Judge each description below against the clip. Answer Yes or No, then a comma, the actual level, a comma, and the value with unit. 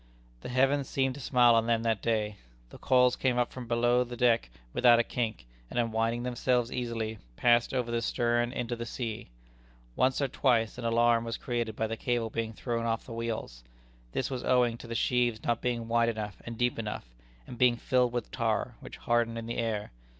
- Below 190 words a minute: No, fast, 205 wpm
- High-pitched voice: No, low, 120 Hz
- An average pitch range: No, narrow, 1.3 semitones